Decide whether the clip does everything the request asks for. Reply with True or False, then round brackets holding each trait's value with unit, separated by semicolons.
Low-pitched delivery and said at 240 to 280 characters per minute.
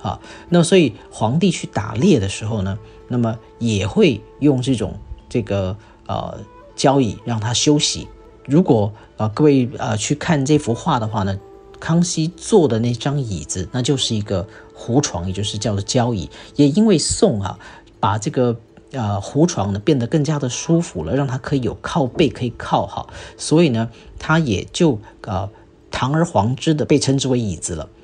True (120 Hz; 250 characters per minute)